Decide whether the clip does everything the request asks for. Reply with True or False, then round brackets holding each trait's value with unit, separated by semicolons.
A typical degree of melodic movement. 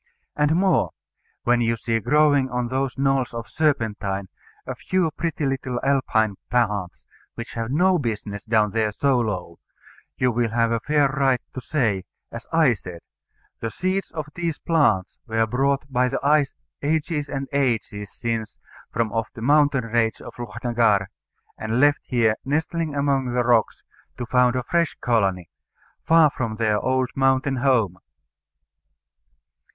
True (4.0 semitones)